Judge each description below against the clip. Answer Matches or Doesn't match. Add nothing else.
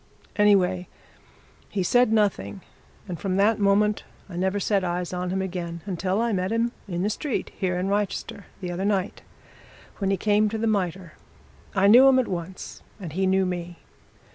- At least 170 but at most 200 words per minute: Matches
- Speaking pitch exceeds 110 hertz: Matches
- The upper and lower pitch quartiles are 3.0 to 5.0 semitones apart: Doesn't match